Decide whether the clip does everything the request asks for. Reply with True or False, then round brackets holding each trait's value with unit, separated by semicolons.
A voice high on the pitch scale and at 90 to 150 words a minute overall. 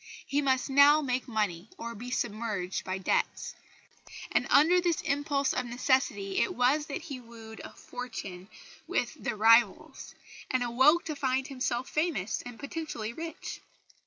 True (250 Hz; 145 wpm)